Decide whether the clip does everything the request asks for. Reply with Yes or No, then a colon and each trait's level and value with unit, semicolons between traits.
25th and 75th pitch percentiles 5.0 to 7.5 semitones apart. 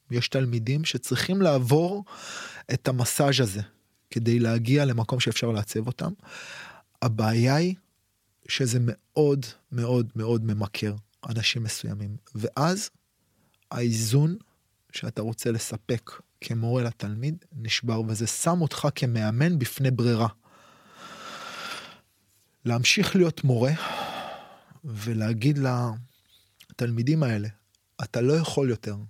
No: average, 4.0 semitones